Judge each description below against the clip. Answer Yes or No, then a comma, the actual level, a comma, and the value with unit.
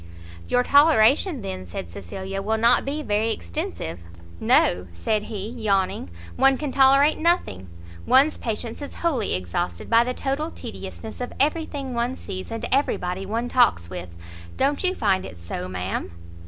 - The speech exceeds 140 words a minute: Yes, average, 160 wpm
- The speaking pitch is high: Yes, high, 225 Hz